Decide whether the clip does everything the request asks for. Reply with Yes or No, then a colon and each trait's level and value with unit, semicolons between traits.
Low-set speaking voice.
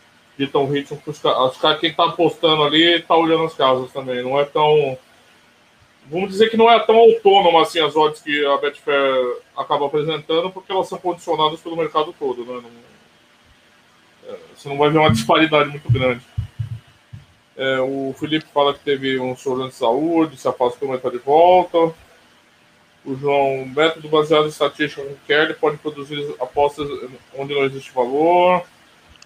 No: medium, 150 Hz